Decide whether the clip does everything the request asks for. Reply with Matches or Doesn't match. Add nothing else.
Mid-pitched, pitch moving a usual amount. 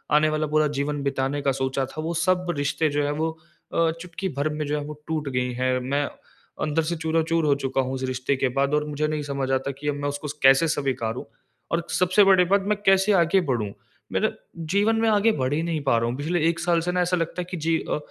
Matches